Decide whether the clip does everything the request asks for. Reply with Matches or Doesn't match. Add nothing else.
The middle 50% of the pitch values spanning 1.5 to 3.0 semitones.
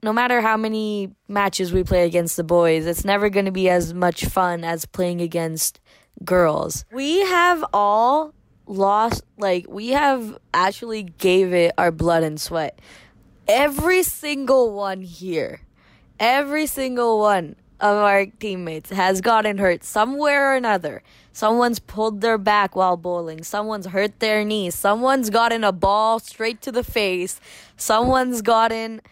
Doesn't match